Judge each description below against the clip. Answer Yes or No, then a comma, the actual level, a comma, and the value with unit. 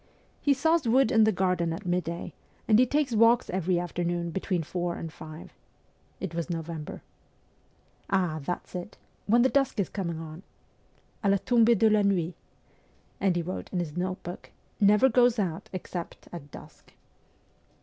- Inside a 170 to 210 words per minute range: Yes, average, 180 wpm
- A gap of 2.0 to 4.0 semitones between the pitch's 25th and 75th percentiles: No, average, 4.6 semitones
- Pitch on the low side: No, medium, 185 Hz